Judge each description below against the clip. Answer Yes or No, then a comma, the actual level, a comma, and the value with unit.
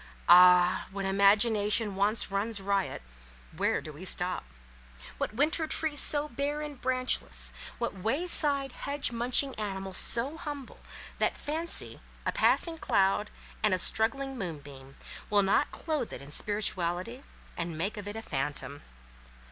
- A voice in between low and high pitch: No, high, 215 Hz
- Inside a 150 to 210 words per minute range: No, average, 140 wpm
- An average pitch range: No, wide, 6.4 semitones